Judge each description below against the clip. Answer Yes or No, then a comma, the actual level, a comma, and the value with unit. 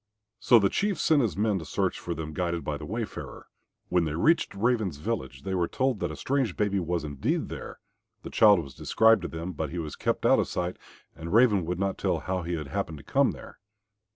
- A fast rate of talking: Yes, fast, 230 wpm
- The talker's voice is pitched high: No, very low, 90 Hz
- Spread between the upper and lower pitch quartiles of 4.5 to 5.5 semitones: Yes, average, 5.2 semitones